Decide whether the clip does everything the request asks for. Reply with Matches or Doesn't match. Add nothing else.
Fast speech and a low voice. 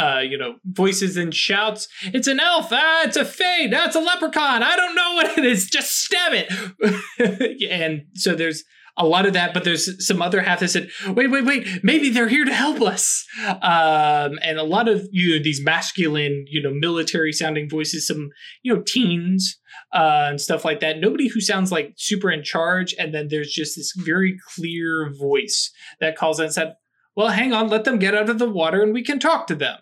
Doesn't match